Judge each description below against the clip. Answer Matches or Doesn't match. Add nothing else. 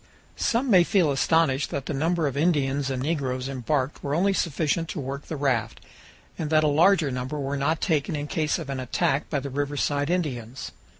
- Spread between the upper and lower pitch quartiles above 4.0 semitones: Doesn't match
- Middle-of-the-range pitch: Matches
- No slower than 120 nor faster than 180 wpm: Doesn't match